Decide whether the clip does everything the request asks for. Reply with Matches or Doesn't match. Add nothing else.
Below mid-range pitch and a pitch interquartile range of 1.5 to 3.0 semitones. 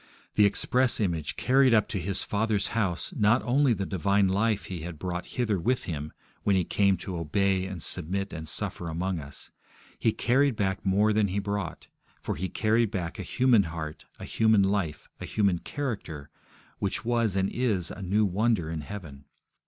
Doesn't match